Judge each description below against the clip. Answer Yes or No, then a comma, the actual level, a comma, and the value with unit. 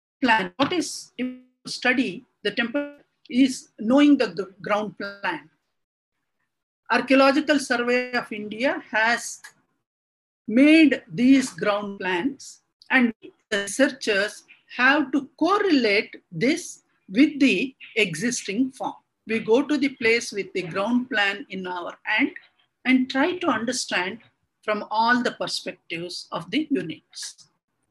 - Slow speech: Yes, slow, 115 wpm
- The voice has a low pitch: No, very high, 250 Hz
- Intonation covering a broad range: No, average, 4.8 semitones